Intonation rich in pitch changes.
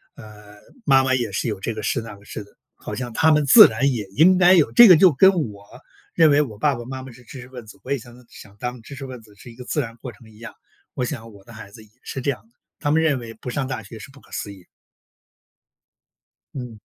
No: average, 4.2 semitones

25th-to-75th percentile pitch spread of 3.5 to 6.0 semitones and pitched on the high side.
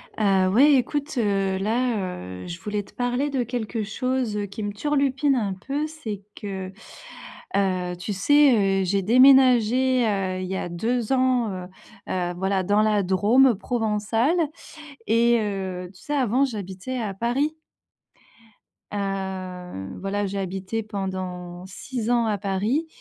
Yes: average, 4.5 semitones; high, 210 Hz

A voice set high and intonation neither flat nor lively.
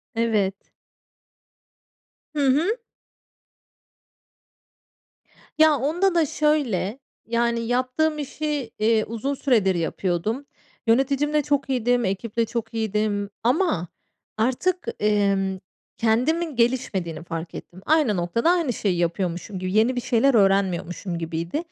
No: high, 230 Hz; wide, 6.2 semitones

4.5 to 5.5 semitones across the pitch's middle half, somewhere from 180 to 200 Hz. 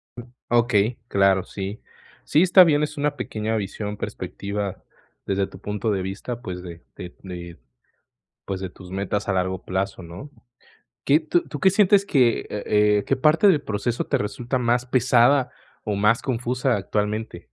No: average, 4.8 semitones; low, 110 Hz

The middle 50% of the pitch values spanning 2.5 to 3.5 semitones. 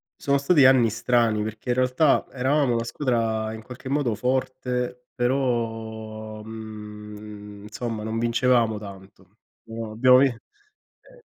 Yes: average, 2.8 semitones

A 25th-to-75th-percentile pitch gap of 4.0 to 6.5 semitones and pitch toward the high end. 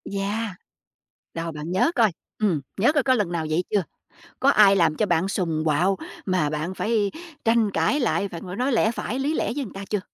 Yes: average, 4.7 semitones; high, 195 Hz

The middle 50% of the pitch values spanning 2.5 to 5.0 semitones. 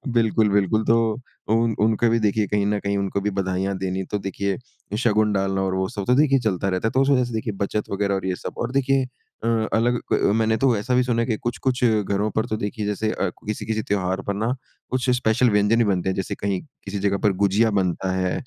Yes: average, 2.9 semitones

